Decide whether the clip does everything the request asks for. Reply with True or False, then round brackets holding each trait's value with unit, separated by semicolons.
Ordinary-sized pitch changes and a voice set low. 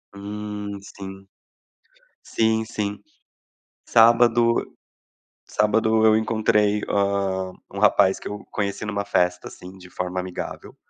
False (2.0 semitones; 105 Hz)